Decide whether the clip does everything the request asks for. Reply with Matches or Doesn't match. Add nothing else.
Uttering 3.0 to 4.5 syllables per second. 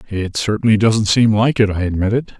Doesn't match